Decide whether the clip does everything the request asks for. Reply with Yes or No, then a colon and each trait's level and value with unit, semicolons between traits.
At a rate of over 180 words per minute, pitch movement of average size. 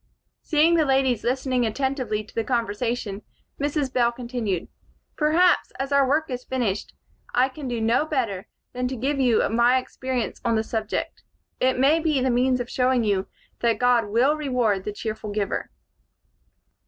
No: average, 165 wpm; average, 3.0 semitones